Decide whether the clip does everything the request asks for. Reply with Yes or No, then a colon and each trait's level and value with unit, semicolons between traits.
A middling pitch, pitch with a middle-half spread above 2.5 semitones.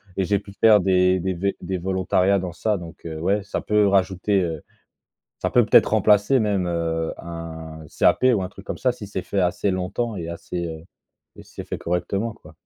No: very low, 95 Hz; average, 2.9 semitones